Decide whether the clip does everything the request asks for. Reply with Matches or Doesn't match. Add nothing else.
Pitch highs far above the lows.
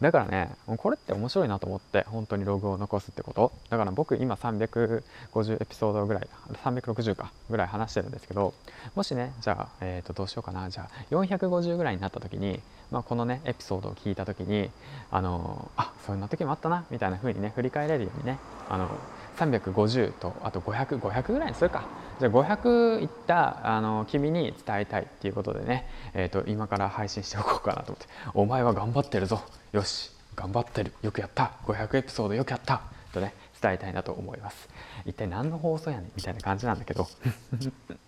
Doesn't match